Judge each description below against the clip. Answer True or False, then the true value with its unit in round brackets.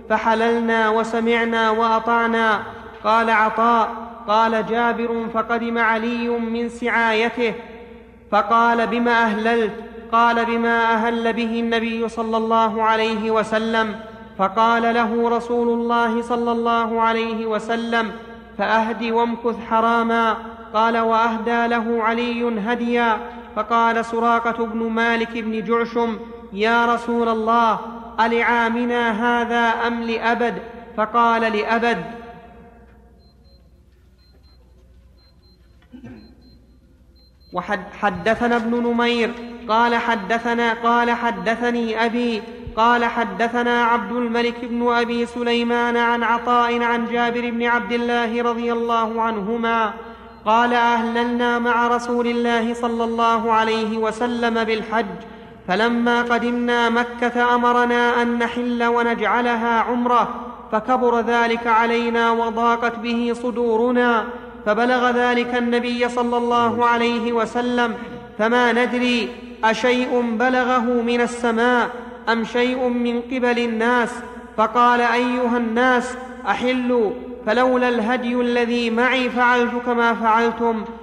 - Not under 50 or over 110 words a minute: True (100 wpm)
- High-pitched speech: True (235 Hz)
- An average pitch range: False (0.9 semitones)